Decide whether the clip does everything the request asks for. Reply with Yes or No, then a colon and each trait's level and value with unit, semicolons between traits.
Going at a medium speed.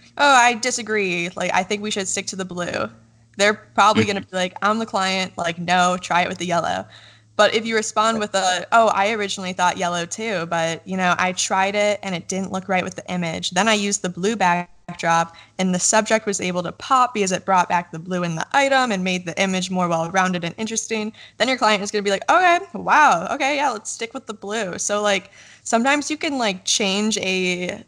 No: fast, 235 wpm